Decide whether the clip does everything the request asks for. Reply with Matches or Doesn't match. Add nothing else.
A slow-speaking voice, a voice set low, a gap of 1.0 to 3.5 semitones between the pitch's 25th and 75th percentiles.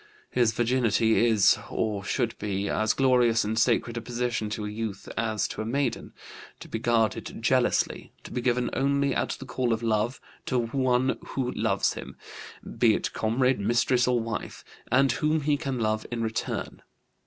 Doesn't match